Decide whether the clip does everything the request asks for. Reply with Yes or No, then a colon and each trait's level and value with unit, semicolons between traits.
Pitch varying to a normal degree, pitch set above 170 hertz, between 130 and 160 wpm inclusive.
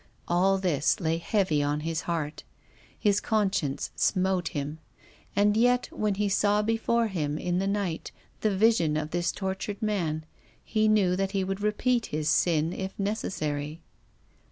Yes: average, 4.5 semitones; high, 190 Hz; average, 155 wpm